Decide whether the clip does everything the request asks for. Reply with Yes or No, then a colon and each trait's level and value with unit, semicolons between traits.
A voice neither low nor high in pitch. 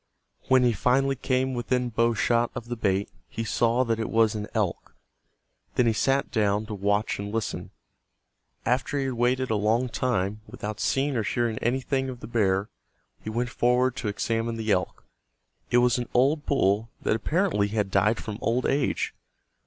No: low, 115 Hz